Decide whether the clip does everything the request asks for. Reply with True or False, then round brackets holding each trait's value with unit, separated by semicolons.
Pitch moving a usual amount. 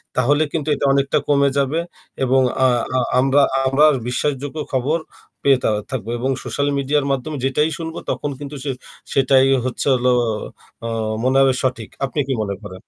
False (1.9 semitones)